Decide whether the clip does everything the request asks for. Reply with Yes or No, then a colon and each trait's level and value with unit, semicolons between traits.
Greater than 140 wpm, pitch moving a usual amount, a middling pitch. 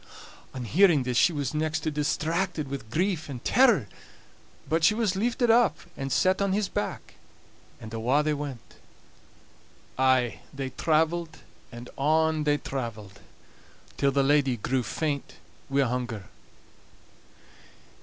No: slow, 135 wpm; average, 4.1 semitones; medium, 145 Hz